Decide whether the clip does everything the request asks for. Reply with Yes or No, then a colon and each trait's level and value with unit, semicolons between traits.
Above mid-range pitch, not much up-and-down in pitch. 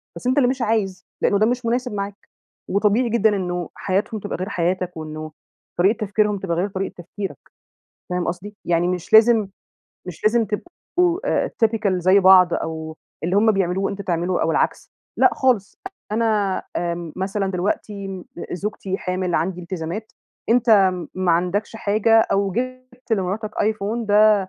No: high, 200 Hz; average, 3.3 semitones